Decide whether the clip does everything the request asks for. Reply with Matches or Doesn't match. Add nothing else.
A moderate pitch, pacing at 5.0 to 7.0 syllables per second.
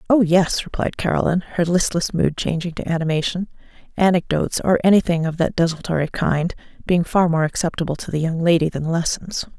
Matches